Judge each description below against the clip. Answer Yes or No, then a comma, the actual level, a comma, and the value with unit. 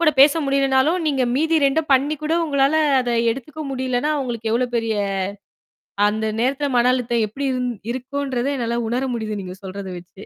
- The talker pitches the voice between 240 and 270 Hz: Yes, very high, 255 Hz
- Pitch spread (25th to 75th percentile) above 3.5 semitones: No, average, 3.2 semitones